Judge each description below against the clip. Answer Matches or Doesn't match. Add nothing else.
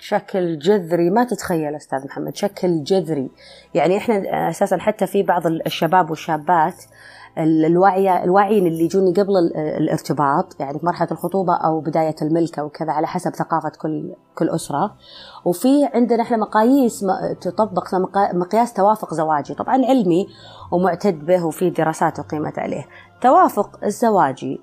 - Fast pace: Doesn't match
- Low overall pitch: Doesn't match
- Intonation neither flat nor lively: Matches